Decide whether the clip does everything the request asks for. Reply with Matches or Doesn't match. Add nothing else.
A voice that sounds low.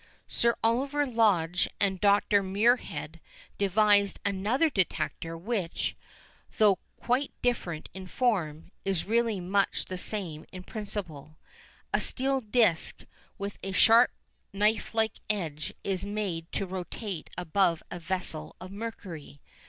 Doesn't match